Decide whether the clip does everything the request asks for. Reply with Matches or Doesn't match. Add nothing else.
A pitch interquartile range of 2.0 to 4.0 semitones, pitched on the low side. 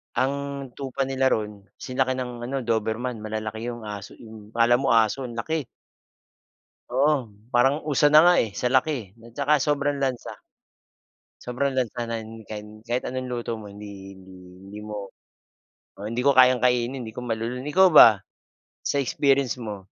Matches